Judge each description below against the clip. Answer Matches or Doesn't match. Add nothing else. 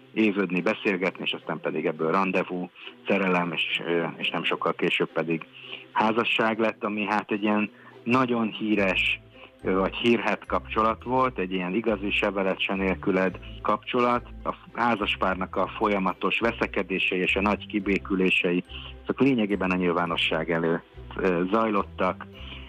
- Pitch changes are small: Doesn't match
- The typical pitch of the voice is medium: Doesn't match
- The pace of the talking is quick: Doesn't match